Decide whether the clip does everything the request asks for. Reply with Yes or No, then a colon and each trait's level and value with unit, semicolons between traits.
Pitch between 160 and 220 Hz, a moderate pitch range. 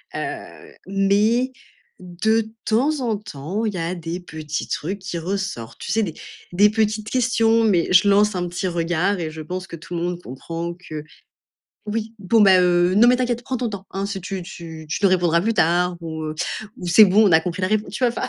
Yes: medium, 185 Hz; average, 4.0 semitones